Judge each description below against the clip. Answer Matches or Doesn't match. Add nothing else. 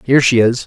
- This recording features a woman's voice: Doesn't match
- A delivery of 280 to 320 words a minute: Doesn't match